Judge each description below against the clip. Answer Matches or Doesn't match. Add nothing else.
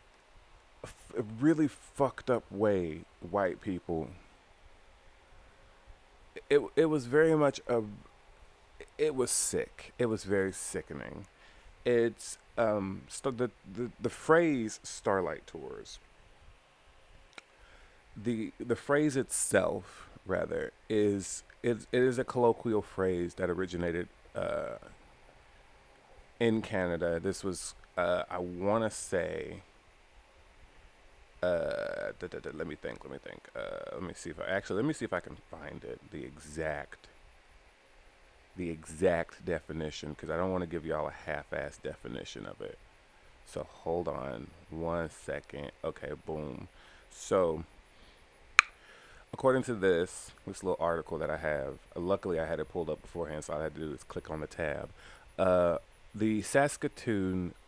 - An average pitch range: Doesn't match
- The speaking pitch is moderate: Doesn't match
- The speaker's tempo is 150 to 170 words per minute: Doesn't match